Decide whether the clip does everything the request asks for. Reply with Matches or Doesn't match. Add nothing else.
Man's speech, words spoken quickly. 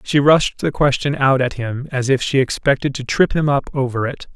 Matches